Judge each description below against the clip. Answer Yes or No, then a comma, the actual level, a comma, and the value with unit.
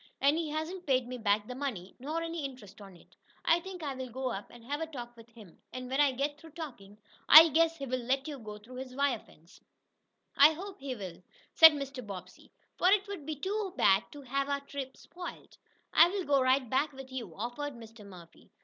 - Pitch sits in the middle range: No, very high, 270 Hz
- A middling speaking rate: No, fast, 215 wpm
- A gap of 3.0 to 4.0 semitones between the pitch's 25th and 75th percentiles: No, average, 4.6 semitones